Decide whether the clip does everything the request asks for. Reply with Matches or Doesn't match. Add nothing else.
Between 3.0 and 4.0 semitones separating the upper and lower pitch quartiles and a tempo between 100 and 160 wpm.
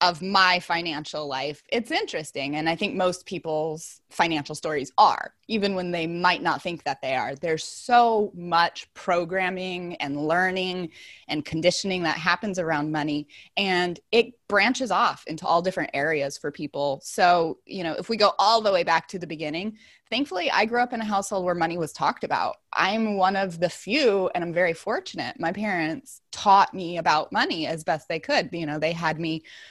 Doesn't match